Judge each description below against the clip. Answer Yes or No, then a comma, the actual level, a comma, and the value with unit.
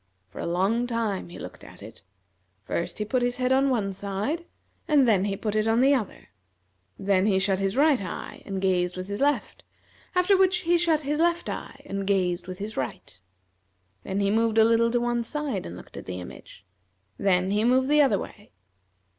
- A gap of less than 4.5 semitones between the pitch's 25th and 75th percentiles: No, wide, 5.4 semitones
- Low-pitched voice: No, high, 215 Hz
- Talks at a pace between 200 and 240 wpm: Yes, fast, 205 wpm